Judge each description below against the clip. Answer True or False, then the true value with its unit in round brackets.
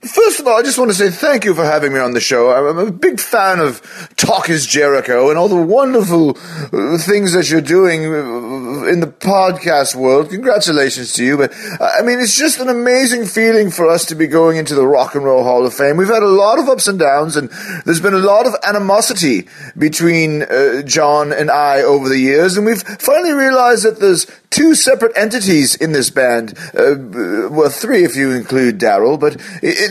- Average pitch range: False (7.7 semitones)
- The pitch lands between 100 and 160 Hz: False (170 Hz)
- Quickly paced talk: True (210 wpm)